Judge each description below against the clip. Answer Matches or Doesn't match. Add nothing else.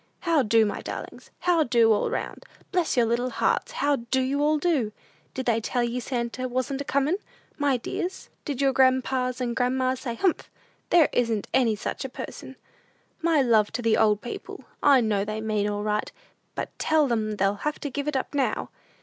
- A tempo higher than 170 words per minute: Matches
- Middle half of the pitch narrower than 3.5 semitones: Doesn't match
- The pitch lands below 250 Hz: Doesn't match